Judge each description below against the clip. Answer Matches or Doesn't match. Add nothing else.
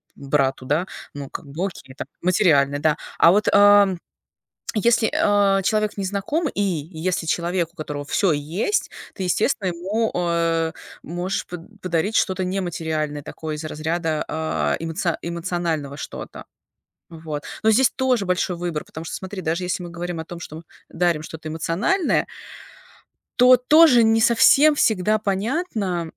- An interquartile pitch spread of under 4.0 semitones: Doesn't match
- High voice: Doesn't match